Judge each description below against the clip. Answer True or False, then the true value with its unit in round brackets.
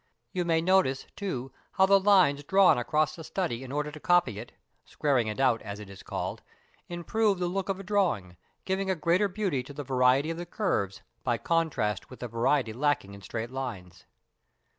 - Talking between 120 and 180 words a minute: False (195 wpm)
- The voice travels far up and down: True (7.1 semitones)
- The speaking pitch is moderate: True (145 Hz)